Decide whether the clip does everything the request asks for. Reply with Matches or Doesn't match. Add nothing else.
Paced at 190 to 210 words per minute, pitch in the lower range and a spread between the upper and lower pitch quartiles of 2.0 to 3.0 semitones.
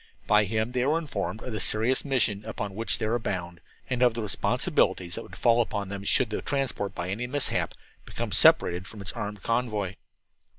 Doesn't match